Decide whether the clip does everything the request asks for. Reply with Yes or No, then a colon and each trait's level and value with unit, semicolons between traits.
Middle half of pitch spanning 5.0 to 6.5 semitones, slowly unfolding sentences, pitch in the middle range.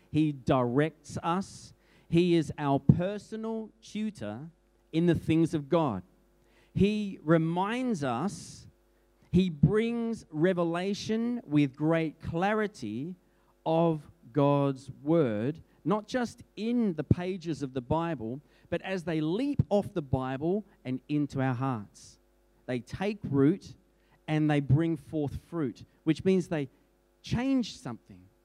Yes: average, 5.3 semitones; slow, 120 wpm; medium, 160 Hz